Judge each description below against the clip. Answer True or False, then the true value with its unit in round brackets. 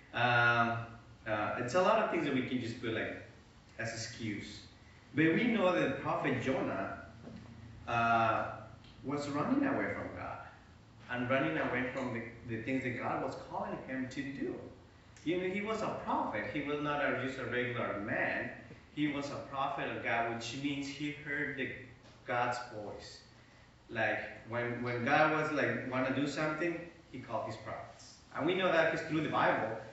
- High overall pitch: False (125 Hz)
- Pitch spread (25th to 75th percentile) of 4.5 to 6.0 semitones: False (3.8 semitones)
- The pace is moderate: True (180 wpm)